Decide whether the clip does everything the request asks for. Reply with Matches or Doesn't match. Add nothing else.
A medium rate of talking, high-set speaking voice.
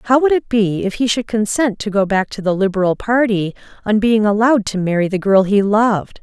Doesn't match